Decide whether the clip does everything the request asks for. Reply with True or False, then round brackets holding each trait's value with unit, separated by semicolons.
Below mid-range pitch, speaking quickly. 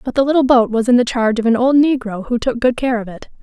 False (240 Hz; 315 wpm)